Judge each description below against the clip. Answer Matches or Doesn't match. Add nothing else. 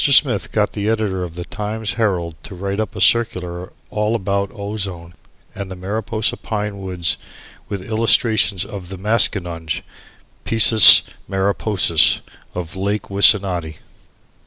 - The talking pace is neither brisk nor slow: Doesn't match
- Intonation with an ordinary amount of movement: Matches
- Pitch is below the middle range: Matches